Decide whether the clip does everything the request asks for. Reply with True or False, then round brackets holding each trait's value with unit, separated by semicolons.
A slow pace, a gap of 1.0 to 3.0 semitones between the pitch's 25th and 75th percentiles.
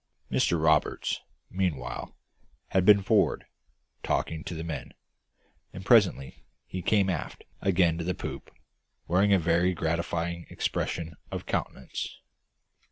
True (120 wpm; 2.7 semitones)